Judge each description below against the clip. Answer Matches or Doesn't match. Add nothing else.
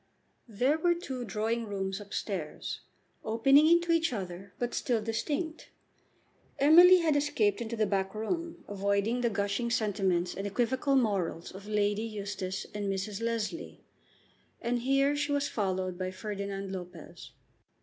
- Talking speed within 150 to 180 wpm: Doesn't match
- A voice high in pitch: Matches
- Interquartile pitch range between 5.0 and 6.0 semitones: Matches